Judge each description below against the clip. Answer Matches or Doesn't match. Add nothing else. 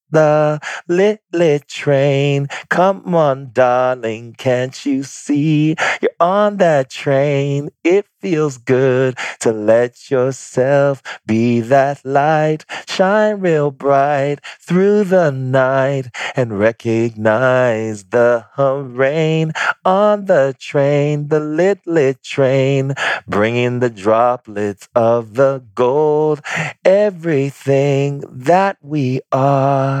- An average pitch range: Matches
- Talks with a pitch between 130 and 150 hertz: Matches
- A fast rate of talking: Doesn't match